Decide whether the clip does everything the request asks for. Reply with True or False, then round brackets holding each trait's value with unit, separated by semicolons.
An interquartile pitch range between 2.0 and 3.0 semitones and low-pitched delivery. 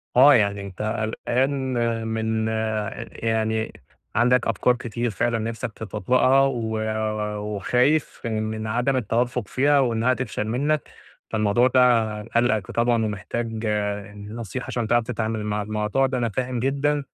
True (2.5 semitones; 115 Hz)